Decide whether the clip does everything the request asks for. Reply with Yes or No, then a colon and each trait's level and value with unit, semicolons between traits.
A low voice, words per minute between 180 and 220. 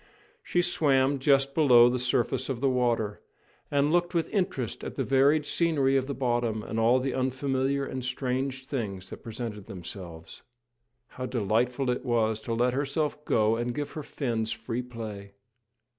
No: low, 125 Hz; average, 165 wpm